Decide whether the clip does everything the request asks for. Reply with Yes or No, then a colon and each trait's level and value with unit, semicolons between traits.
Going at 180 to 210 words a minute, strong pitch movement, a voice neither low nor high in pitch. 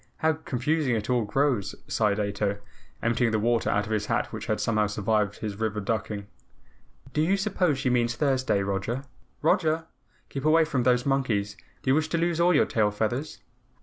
No: average, 185 wpm; wide, 5.7 semitones; low, 120 Hz